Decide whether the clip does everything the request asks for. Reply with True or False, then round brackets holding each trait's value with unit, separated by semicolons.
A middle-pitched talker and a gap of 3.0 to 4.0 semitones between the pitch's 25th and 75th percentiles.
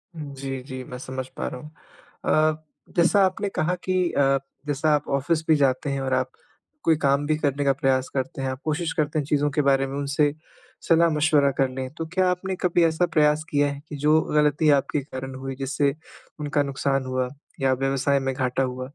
False (145 Hz; 2.6 semitones)